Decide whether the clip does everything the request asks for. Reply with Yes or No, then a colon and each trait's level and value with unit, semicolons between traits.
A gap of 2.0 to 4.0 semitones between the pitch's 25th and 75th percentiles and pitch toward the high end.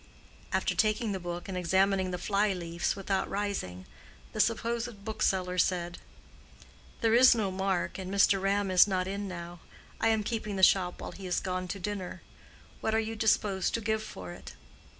Yes: average, 2.7 semitones; high, 195 Hz